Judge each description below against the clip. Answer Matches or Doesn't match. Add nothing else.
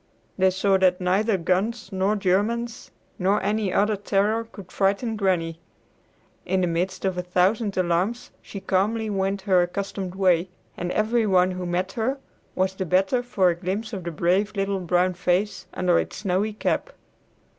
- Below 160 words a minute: Doesn't match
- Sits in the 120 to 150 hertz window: Doesn't match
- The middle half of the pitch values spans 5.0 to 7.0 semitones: Doesn't match